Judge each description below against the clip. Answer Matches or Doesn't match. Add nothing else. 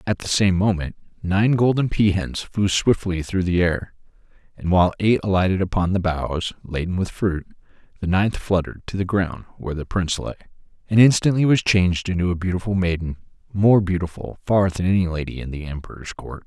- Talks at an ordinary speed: Matches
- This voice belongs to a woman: Doesn't match